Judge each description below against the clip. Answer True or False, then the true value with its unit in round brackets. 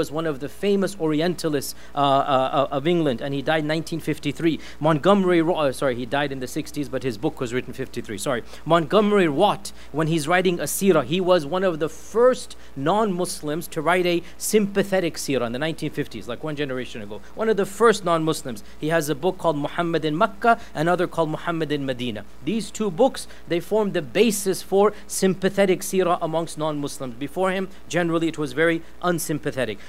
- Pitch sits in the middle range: True (165 Hz)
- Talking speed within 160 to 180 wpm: False (190 wpm)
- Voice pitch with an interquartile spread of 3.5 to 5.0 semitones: True (4.2 semitones)